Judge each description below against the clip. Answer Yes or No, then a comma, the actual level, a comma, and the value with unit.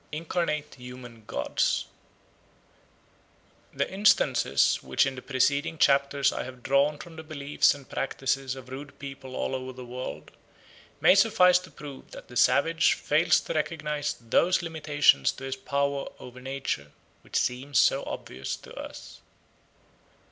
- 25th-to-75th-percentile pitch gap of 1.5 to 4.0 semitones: Yes, average, 2.9 semitones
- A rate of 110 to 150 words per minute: Yes, average, 140 wpm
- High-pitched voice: No, medium, 140 Hz